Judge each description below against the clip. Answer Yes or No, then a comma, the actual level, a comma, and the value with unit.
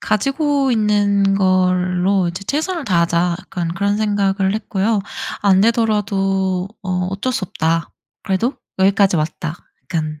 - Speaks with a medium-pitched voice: No, high, 195 Hz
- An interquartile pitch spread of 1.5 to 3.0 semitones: Yes, narrow, 2.5 semitones